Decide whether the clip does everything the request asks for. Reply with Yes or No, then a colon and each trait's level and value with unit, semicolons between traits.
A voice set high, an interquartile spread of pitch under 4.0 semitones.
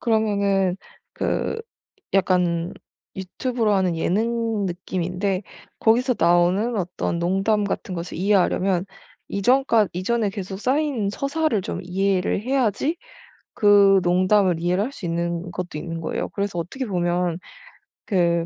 Yes: high, 195 Hz; average, 3.6 semitones